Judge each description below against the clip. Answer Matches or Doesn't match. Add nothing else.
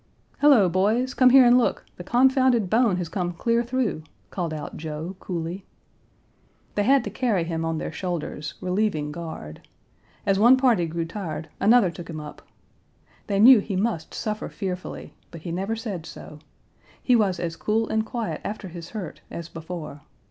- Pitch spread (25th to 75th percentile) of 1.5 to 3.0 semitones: Doesn't match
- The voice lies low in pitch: Doesn't match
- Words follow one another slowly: Doesn't match